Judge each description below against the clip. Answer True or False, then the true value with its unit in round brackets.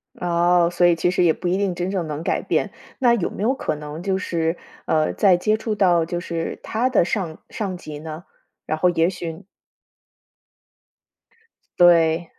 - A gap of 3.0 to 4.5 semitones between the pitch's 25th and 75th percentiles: False (2.6 semitones)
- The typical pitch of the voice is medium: True (175 Hz)